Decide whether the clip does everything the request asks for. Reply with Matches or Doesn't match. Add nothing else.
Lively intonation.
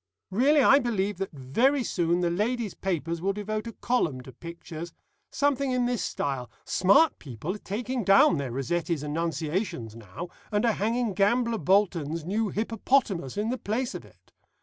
Matches